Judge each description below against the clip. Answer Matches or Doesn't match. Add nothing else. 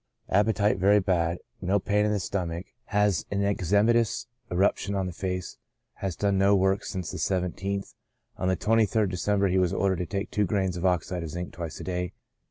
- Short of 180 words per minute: Doesn't match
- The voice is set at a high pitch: Doesn't match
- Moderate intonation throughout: Doesn't match